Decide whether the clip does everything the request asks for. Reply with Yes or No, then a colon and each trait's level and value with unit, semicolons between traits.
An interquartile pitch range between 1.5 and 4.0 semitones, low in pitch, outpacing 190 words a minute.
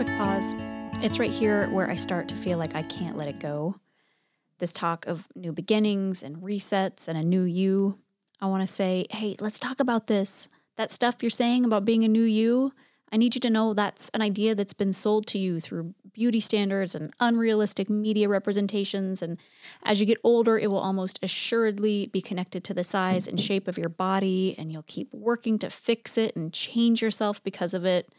No: average, 3.0 semitones; high, 200 Hz; fast, 205 wpm